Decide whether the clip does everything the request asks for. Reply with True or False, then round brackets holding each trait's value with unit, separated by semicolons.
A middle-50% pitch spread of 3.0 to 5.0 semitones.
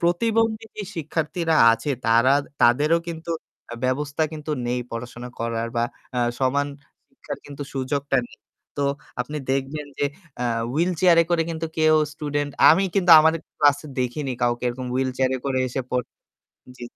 True (4.0 semitones)